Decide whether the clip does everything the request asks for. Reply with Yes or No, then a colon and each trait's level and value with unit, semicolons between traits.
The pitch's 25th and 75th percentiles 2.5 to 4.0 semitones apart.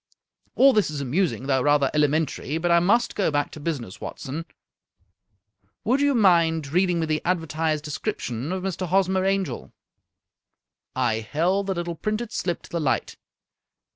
No: average, 4.4 semitones